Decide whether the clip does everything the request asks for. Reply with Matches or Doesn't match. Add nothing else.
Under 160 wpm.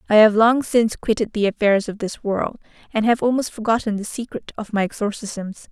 Doesn't match